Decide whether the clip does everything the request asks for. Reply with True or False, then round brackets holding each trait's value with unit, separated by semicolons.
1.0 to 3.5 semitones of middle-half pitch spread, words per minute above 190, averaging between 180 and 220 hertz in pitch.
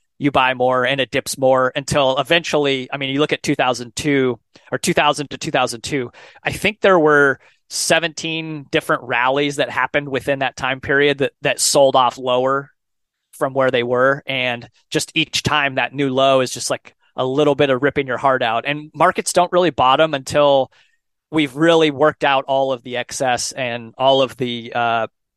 False (2.6 semitones; 200 wpm; 135 Hz)